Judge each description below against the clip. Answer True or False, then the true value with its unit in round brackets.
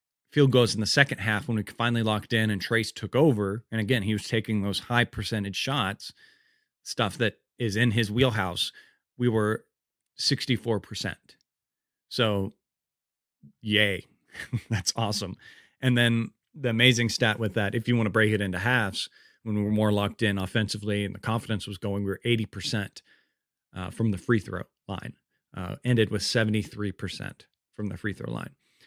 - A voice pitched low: True (110 Hz)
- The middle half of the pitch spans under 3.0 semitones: True (2.5 semitones)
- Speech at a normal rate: True (170 wpm)